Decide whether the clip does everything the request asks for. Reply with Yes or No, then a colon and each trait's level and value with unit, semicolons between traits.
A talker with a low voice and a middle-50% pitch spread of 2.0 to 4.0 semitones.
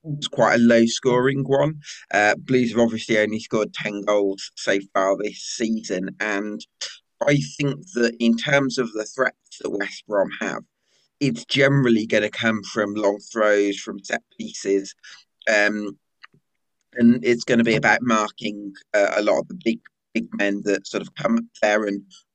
Yes: low, 110 Hz; average, 3.1 semitones